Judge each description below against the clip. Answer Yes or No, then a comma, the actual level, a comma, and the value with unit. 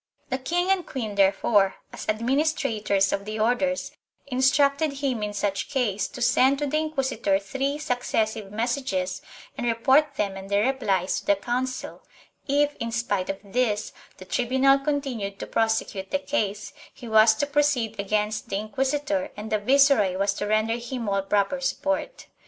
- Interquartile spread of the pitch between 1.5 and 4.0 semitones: No, average, 5.0 semitones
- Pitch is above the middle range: Yes, high, 235 Hz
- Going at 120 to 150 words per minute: No, average, 165 wpm